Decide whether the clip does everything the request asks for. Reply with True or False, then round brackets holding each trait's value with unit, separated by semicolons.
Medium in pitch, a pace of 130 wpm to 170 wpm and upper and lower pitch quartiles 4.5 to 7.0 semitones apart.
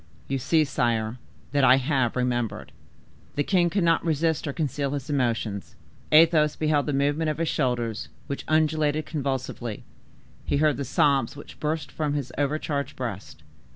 False (145 Hz; 160 wpm; 3.4 semitones)